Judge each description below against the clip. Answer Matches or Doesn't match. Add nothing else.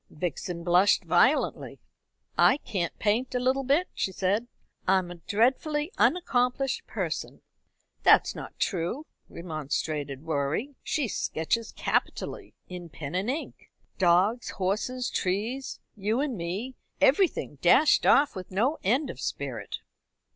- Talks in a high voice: Matches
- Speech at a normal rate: Doesn't match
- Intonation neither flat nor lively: Doesn't match